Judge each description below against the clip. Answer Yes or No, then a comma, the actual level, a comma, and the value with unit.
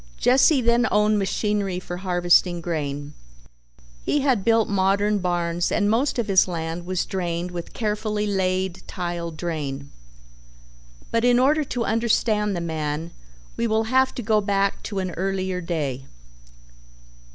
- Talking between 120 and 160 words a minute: Yes, average, 140 wpm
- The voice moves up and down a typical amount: Yes, average, 4.0 semitones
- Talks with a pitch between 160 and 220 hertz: Yes, high, 190 Hz